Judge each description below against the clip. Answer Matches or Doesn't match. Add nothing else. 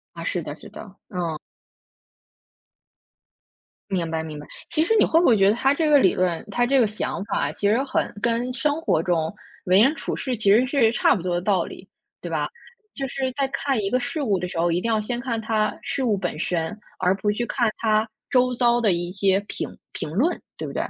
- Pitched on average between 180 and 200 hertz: Doesn't match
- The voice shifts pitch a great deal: Matches